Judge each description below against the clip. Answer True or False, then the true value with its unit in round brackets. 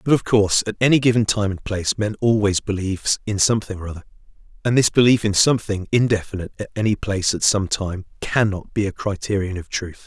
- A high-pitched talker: False (105 Hz)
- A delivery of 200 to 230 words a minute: True (205 wpm)